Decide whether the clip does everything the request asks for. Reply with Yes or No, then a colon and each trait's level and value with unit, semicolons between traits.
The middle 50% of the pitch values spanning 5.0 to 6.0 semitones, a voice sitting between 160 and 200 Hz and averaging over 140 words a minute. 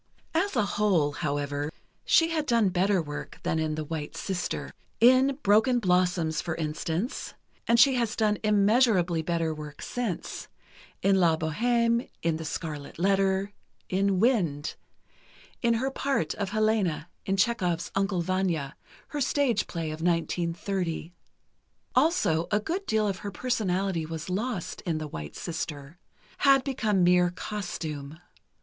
No: average, 5.3 semitones; medium, 185 Hz; slow, 135 wpm